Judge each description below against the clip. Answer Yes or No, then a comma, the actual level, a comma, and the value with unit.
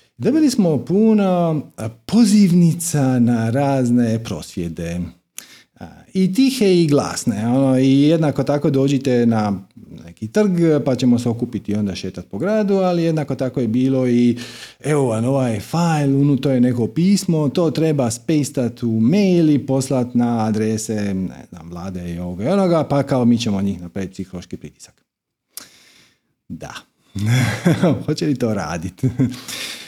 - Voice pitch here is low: Yes, low, 130 Hz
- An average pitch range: No, wide, 6.3 semitones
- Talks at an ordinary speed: Yes, average, 140 wpm